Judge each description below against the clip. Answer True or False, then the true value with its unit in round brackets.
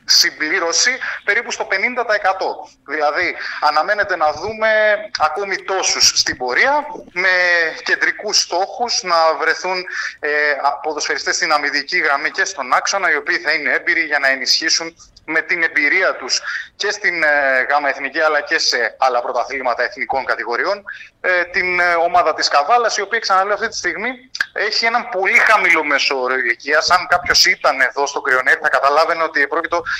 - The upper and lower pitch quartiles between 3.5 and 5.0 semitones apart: False (5.6 semitones)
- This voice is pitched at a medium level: True (175 Hz)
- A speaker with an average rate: True (150 wpm)